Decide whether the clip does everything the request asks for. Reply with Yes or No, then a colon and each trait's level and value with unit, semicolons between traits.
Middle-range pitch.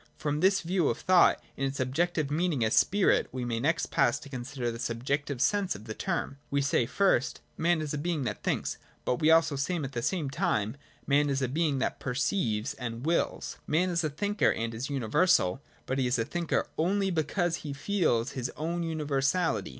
Yes: medium, 145 Hz